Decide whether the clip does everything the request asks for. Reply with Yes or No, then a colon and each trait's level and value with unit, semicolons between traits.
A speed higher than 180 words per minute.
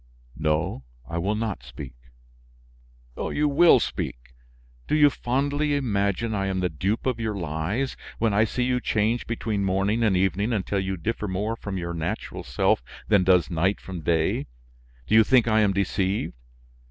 No: average, 165 wpm